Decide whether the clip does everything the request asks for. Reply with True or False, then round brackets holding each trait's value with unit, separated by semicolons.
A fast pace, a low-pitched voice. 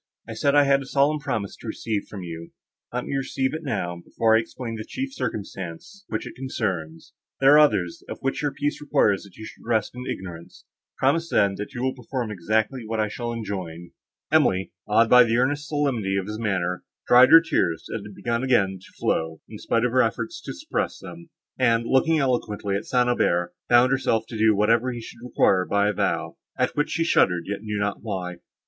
True (210 wpm; 115 Hz)